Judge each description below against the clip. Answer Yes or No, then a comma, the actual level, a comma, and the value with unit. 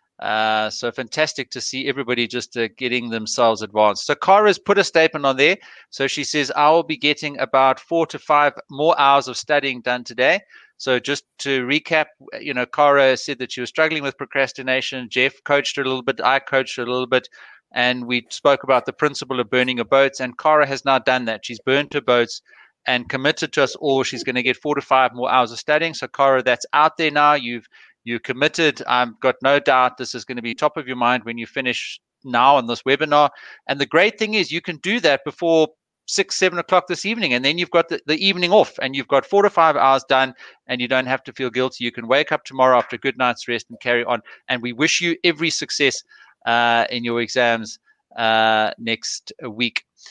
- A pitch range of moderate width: Yes, average, 3.3 semitones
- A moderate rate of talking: No, fast, 230 wpm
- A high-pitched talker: No, low, 135 Hz